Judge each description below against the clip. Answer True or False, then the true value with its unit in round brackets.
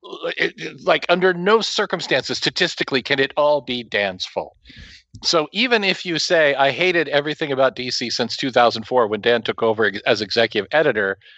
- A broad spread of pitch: True (6.4 semitones)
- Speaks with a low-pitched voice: False (150 Hz)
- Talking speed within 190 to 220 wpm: False (160 wpm)